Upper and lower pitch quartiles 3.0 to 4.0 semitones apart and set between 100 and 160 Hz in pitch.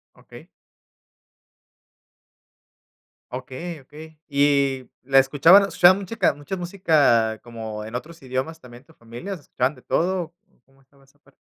No: average, 4.5 semitones; medium, 140 Hz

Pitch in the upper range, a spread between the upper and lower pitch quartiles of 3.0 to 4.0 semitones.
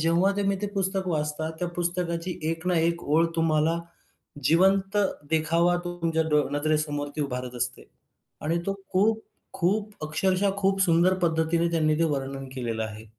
No: medium, 165 Hz; average, 3.3 semitones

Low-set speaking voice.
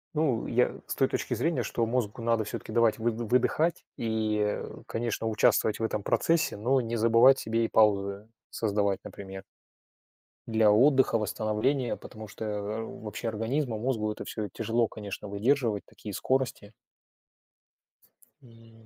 Yes: low, 115 Hz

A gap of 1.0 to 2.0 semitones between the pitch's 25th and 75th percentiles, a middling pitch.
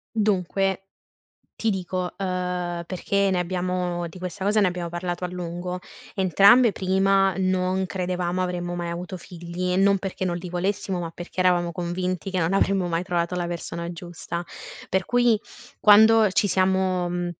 Yes: narrow, 1.6 semitones; medium, 180 Hz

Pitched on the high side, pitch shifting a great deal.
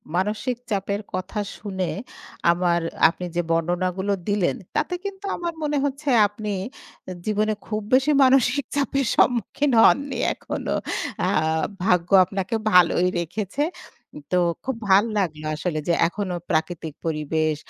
Yes: high, 200 Hz; wide, 6.1 semitones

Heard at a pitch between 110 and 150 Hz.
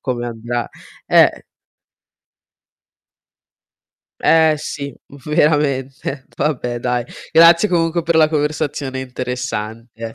Yes: low, 135 Hz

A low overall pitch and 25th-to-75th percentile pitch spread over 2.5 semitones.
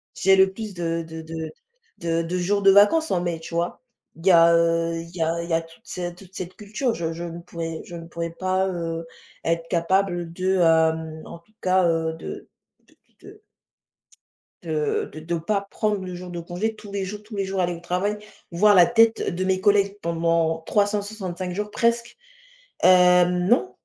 No: medium, 180 Hz; average, 2.9 semitones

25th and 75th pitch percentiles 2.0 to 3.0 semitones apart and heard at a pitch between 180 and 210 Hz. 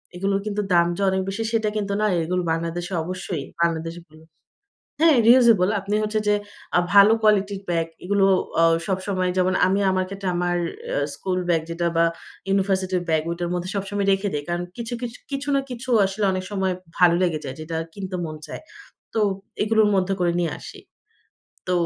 Yes: narrow, 2.6 semitones; high, 190 Hz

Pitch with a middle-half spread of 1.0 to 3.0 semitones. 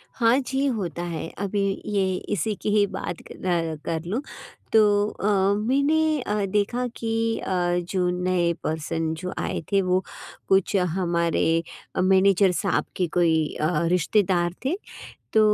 No: average, 3.5 semitones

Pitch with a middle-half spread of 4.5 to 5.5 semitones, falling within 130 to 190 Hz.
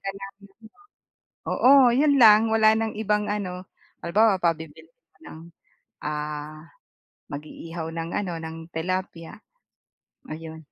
Yes: average, 5.1 semitones; medium, 185 Hz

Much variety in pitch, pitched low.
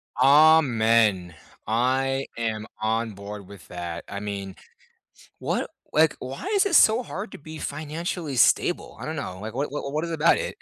Yes: wide, 6.9 semitones; low, 130 Hz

